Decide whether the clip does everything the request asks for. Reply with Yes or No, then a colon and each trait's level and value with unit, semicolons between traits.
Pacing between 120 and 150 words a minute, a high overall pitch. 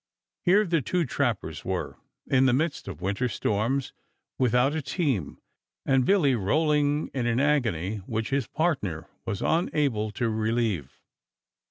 No: average, 140 wpm; low, 125 Hz